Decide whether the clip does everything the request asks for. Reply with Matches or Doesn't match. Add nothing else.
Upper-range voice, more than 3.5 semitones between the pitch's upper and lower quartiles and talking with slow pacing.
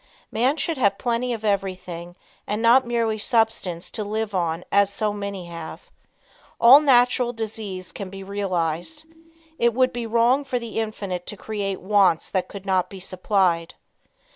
Doesn't match